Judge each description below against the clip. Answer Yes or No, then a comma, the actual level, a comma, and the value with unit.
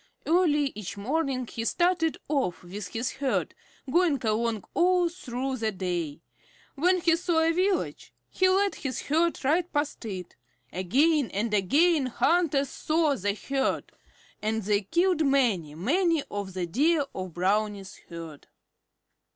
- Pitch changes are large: Yes, wide, 8.3 semitones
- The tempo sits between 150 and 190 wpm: No, average, 140 wpm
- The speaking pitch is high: Yes, very high, 270 Hz